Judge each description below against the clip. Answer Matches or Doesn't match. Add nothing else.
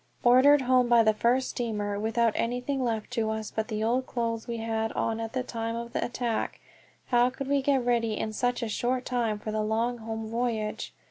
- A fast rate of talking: Matches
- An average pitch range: Doesn't match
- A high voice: Matches